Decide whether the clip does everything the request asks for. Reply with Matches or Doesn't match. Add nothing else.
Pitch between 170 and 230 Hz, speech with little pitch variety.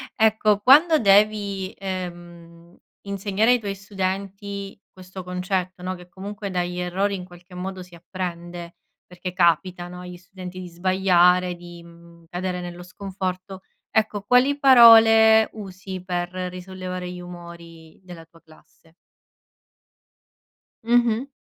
Matches